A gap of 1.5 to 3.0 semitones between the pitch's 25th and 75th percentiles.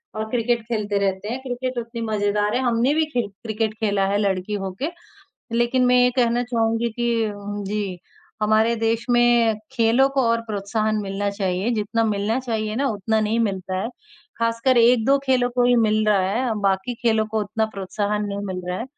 Yes: average, 2.7 semitones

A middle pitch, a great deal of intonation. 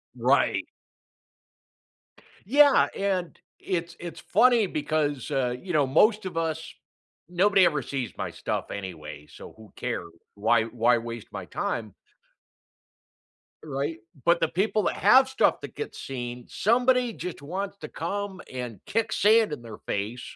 Yes: medium, 160 Hz; wide, 8.5 semitones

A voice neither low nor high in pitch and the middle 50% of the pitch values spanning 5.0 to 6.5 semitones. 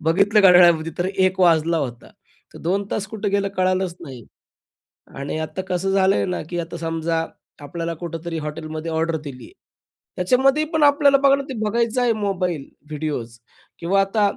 No: medium, 175 Hz; average, 3.7 semitones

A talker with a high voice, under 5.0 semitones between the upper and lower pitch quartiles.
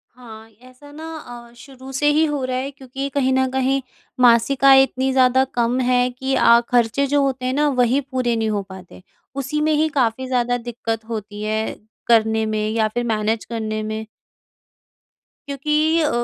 Yes: very high, 255 Hz; average, 3.2 semitones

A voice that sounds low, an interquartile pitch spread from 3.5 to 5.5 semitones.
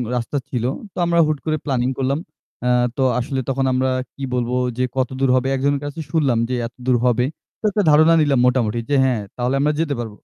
No: low, 130 Hz; narrow, 2.6 semitones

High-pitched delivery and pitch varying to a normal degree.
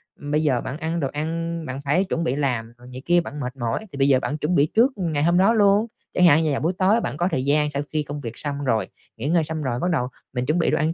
No: medium, 150 Hz; average, 3.8 semitones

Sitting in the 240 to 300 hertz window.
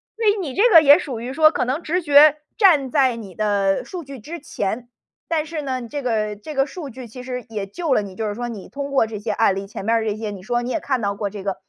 Yes: very high, 250 Hz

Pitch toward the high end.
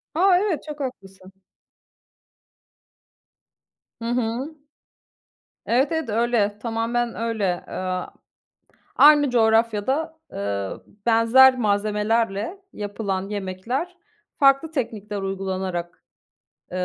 Yes: high, 225 Hz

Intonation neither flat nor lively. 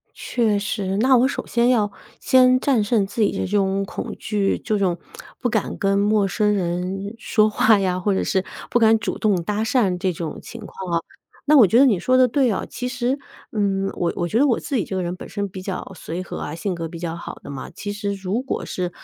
Yes: average, 3.7 semitones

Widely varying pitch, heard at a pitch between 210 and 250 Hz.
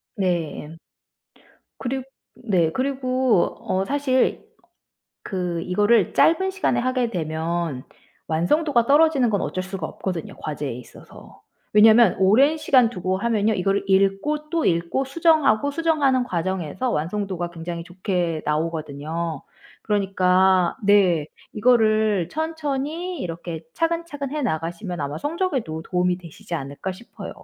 No: wide, 7.3 semitones; high, 195 Hz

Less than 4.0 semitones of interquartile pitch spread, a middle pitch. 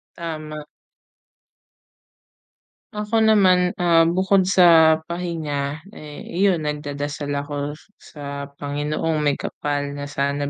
Yes: average, 3.5 semitones; medium, 155 Hz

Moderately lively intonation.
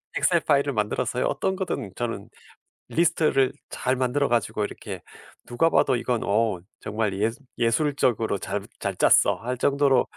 Yes: average, 4.2 semitones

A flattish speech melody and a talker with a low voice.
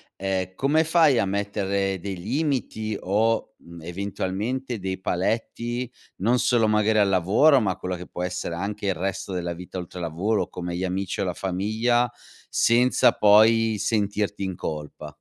No: average, 3.5 semitones; low, 100 Hz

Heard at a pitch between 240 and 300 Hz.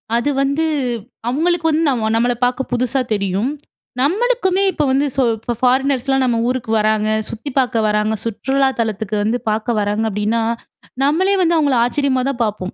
Yes: very high, 250 Hz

